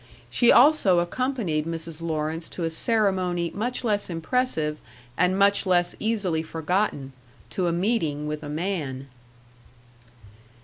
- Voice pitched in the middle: Yes, medium, 175 Hz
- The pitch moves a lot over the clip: No, average, 4.3 semitones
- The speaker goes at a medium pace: No, slow, 125 wpm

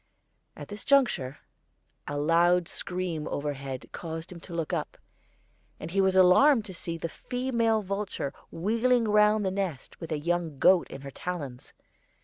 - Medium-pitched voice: Yes, medium, 180 Hz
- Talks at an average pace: Yes, average, 155 wpm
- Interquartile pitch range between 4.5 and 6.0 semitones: Yes, average, 4.8 semitones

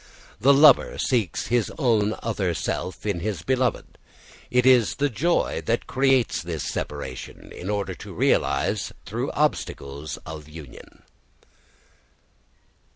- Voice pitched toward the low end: Yes, low, 105 Hz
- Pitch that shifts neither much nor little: No, wide, 7.5 semitones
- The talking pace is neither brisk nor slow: No, slow, 120 wpm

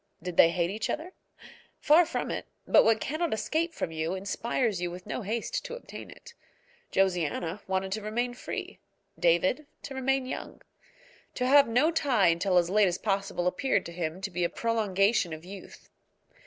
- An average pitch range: No, wide, 6.1 semitones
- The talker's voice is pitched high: Yes, high, 200 Hz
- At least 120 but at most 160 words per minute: No, average, 180 wpm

